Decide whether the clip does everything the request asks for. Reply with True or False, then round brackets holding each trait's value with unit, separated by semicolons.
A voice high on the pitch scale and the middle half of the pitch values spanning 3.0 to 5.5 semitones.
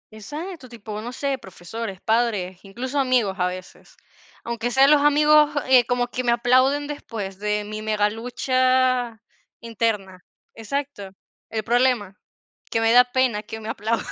True (235 Hz; 3.5 semitones)